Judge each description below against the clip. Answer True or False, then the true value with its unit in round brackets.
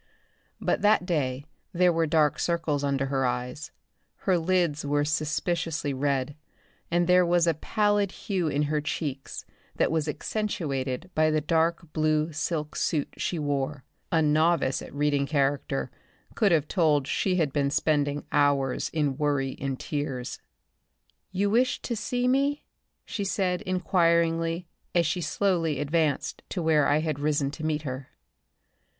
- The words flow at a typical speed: True (150 wpm)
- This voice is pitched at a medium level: True (155 Hz)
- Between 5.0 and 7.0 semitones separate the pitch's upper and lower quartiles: False (3.3 semitones)